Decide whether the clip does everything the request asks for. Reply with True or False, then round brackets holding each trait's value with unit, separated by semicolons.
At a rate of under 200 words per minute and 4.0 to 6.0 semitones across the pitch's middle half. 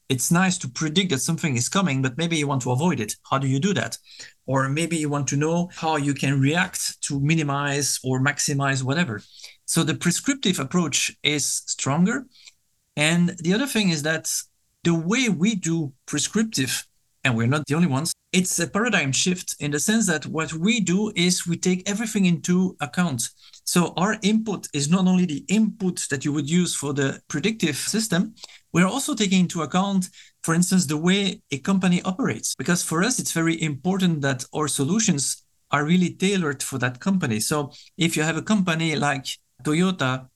True (185 wpm; 4.6 semitones)